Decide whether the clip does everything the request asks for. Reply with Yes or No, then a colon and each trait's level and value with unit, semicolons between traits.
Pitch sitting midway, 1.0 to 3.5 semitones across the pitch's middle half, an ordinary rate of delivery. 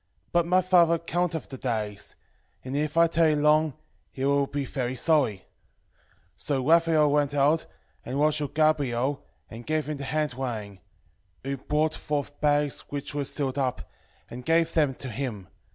Yes: medium, 145 Hz; average, 2.9 semitones; average, 170 wpm